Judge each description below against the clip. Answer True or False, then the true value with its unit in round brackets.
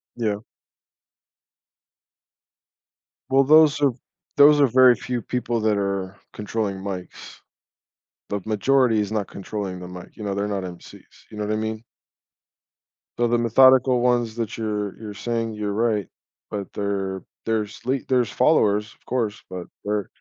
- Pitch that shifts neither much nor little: True (3.2 semitones)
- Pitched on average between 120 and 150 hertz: False (110 Hz)